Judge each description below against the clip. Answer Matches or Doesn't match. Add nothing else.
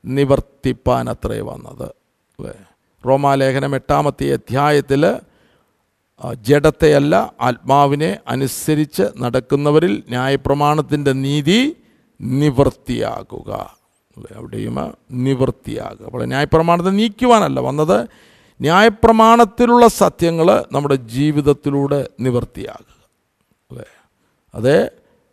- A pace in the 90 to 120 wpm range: Doesn't match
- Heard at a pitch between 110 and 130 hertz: Doesn't match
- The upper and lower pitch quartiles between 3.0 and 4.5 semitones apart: Matches